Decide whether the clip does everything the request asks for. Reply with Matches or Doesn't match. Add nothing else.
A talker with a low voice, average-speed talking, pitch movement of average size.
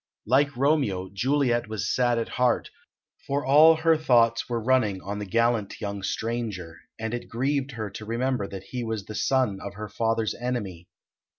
Matches